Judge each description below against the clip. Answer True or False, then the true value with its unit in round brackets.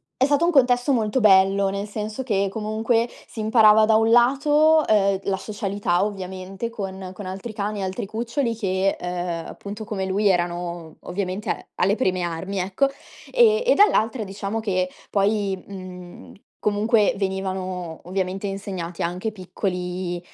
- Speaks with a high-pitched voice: True (200 Hz)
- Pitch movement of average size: True (3.0 semitones)